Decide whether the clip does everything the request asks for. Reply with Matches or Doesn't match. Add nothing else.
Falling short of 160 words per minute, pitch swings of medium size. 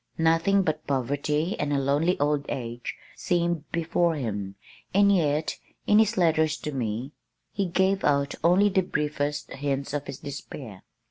Matches